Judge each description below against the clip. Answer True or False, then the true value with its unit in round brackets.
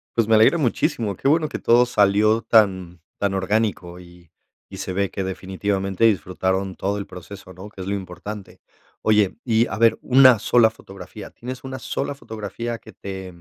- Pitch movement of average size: True (3.3 semitones)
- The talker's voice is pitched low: True (100 Hz)